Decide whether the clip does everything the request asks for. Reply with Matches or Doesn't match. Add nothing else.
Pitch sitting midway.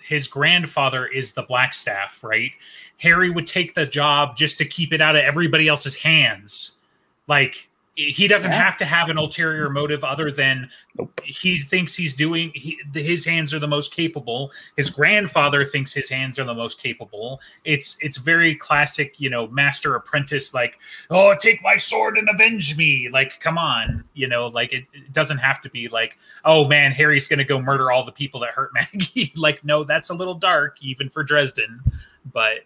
Matches